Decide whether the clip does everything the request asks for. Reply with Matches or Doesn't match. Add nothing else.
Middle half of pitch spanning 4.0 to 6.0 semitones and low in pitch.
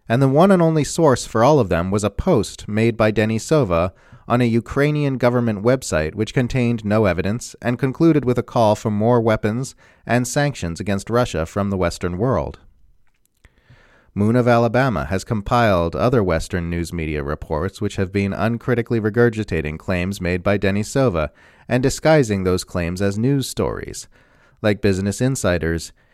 Matches